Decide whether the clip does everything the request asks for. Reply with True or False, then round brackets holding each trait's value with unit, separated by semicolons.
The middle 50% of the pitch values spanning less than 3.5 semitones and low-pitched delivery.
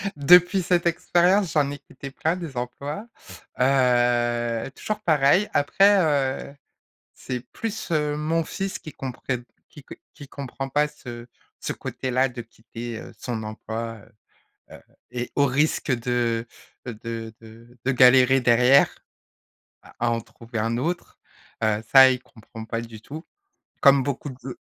False (3.9 semitones; 130 Hz)